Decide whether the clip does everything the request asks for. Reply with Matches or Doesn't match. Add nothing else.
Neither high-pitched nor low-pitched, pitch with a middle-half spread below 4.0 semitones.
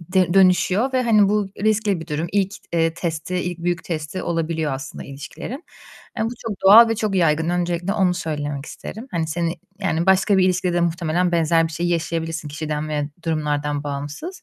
Matches